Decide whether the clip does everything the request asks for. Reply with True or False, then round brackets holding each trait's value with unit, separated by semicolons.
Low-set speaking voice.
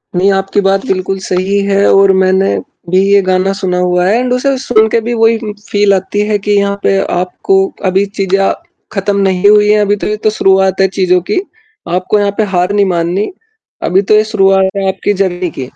False (195 Hz)